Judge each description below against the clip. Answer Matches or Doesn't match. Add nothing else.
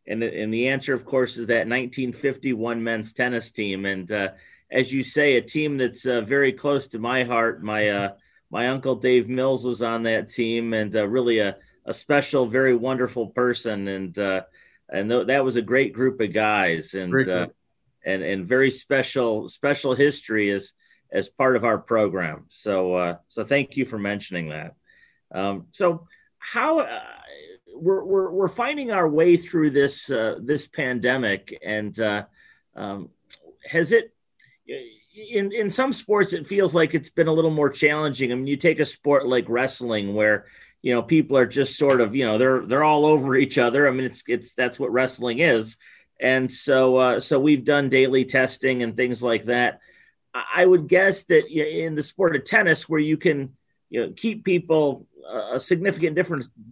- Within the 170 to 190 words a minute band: Matches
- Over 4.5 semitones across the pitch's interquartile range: Matches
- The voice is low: Matches